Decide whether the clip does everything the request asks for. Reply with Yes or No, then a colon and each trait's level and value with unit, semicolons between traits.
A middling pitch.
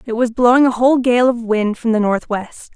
No: high, 235 Hz